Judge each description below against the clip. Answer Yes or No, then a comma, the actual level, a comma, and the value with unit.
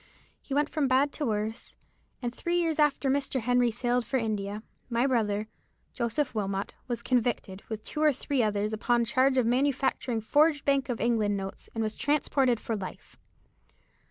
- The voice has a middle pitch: No, high, 245 Hz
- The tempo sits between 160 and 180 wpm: Yes, average, 175 wpm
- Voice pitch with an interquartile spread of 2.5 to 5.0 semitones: Yes, average, 4.0 semitones